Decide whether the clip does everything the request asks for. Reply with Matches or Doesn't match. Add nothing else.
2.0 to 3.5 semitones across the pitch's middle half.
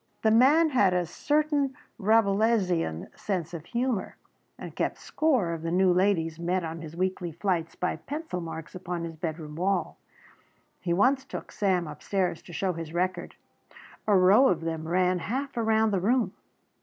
Doesn't match